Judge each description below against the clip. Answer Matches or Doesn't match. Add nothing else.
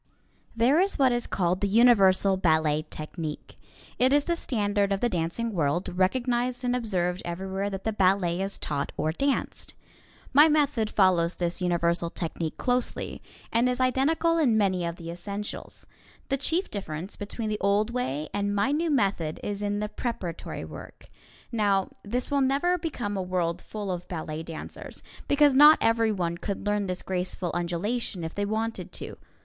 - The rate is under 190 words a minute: Matches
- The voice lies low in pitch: Doesn't match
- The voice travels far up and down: Matches